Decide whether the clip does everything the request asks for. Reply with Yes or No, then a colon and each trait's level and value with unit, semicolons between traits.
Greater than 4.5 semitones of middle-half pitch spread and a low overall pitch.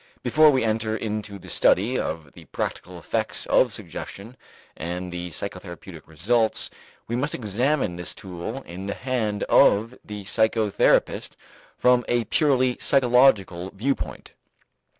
Yes: average, 5.1 semitones; low, 110 Hz